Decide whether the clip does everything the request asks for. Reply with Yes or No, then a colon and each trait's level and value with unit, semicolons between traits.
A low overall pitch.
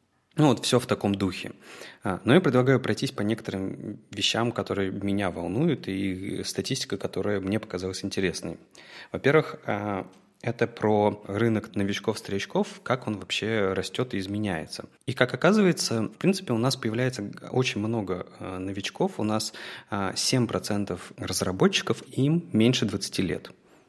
Yes: low, 110 Hz